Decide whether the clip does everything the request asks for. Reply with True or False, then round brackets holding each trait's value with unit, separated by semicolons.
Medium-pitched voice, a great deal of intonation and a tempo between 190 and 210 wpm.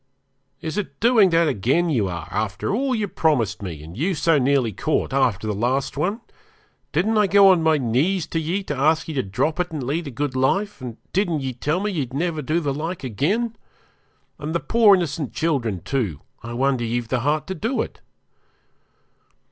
True (150 Hz; 6.2 semitones; 200 wpm)